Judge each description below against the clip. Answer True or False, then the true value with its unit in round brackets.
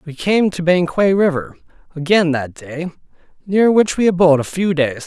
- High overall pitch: False (170 Hz)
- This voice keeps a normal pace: True (180 wpm)